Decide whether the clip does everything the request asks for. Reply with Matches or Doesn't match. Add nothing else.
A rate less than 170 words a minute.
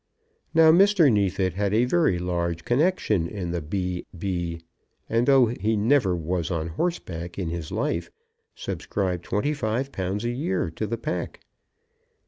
Matches